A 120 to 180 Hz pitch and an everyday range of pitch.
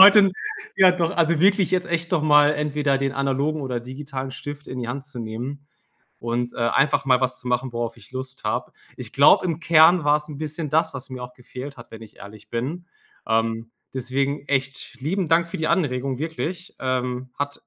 Yes: medium, 140 Hz; average, 3.8 semitones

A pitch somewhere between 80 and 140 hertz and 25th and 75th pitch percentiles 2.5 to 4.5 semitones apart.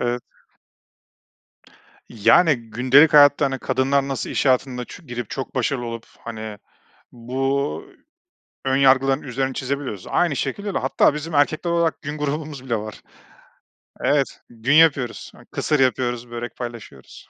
Yes: low, 135 Hz; average, 2.9 semitones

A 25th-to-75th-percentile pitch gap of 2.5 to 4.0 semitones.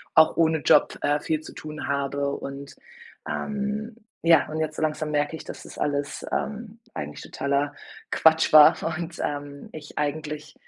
No: narrow, 1.9 semitones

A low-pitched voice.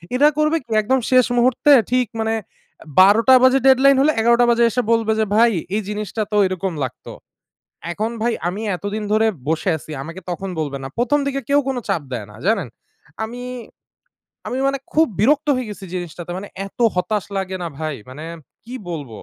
No: high, 220 Hz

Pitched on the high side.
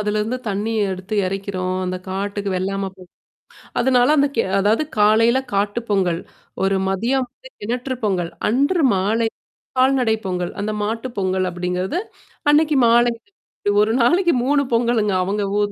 Yes: high, 210 Hz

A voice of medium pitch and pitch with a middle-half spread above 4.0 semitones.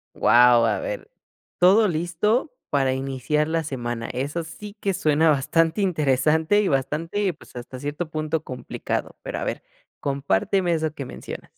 Yes: medium, 155 Hz; average, 4.5 semitones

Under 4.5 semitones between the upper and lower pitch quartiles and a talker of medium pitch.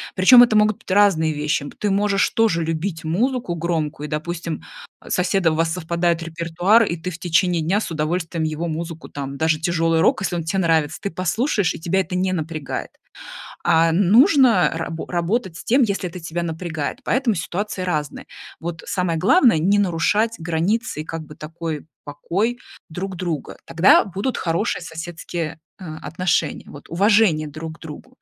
Yes: average, 3.4 semitones; medium, 170 Hz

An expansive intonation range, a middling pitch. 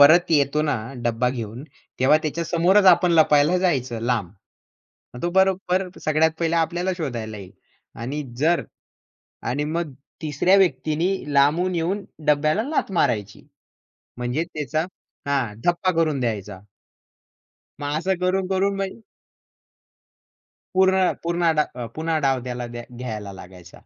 Yes: wide, 6.0 semitones; medium, 150 Hz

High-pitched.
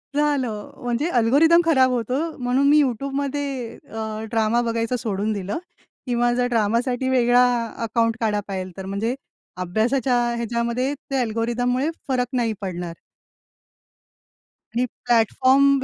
Yes: high, 240 Hz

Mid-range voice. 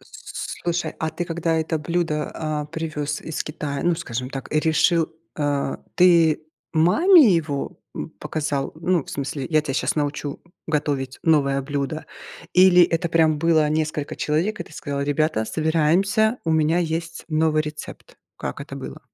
Yes: medium, 155 Hz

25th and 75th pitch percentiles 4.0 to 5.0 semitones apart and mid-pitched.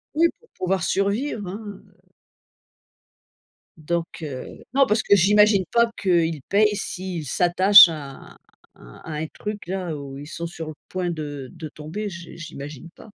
Yes: average, 4.6 semitones; medium, 180 Hz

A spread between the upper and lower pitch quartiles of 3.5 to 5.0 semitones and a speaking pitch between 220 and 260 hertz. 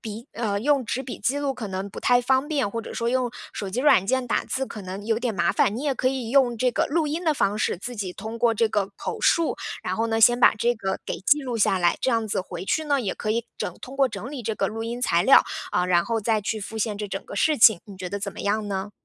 Yes: average, 4.1 semitones; high, 225 Hz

